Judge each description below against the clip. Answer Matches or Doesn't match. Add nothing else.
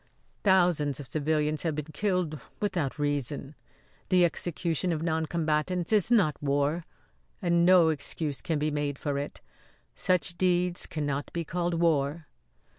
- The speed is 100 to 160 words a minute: Matches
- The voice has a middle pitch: Matches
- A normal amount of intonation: Matches